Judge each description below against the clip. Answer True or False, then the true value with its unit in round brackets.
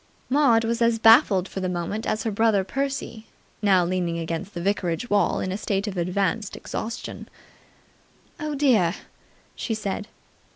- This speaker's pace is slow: False (155 wpm)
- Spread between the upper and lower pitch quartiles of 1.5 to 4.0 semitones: True (3.6 semitones)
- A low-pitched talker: False (205 Hz)